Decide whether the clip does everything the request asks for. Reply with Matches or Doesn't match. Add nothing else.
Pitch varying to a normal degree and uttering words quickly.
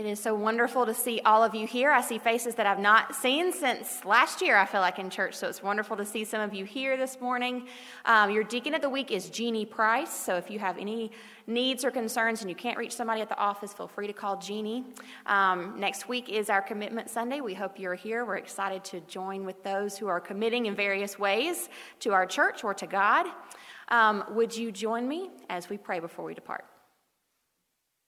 Matches